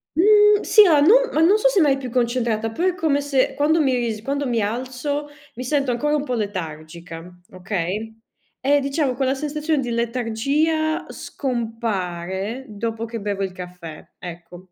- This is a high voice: Yes, high, 245 Hz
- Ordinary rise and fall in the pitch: No, wide, 6.1 semitones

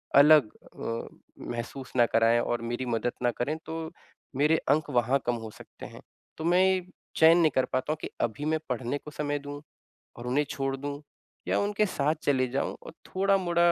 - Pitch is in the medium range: Yes, medium, 145 Hz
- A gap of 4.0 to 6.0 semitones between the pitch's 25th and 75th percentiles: Yes, average, 4.5 semitones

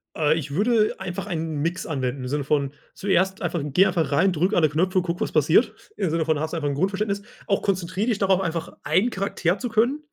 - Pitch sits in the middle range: Yes, medium, 175 Hz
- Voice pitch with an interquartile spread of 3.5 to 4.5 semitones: Yes, average, 4.0 semitones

